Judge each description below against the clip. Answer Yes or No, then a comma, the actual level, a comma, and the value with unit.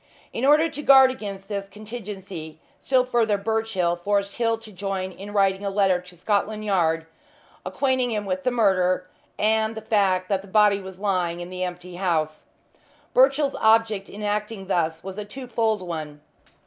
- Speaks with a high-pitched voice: Yes, high, 200 Hz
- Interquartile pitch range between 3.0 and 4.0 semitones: Yes, average, 3.3 semitones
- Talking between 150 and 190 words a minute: Yes, average, 170 wpm